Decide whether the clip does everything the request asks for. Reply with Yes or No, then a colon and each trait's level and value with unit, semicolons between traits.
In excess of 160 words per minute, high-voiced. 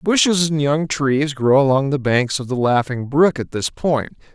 No: fast, 205 wpm; medium, 140 Hz